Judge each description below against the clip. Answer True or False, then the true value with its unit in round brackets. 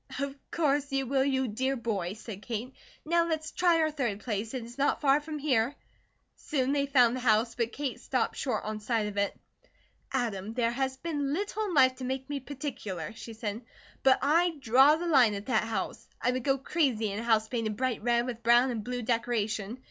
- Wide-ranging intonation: False (3.8 semitones)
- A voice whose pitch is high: True (250 Hz)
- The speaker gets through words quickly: True (210 wpm)